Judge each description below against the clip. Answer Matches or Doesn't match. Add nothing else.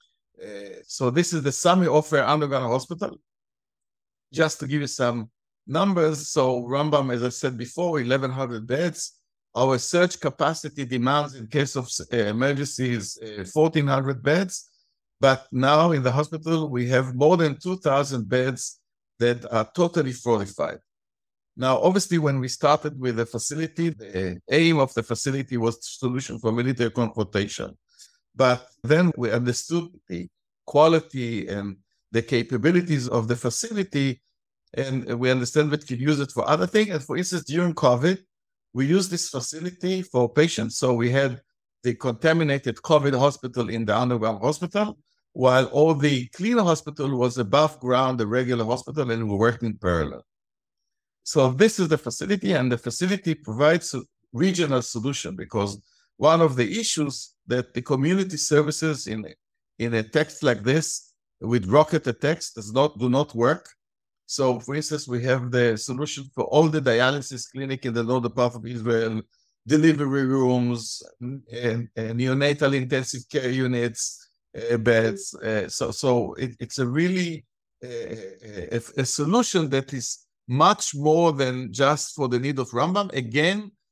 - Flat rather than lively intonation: Doesn't match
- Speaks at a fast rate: Doesn't match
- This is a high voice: Doesn't match